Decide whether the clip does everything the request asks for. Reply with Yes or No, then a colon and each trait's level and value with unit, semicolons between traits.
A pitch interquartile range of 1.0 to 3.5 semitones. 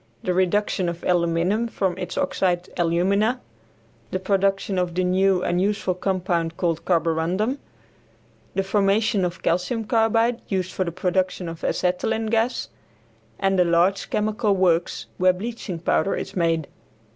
Yes: average, 2.8 semitones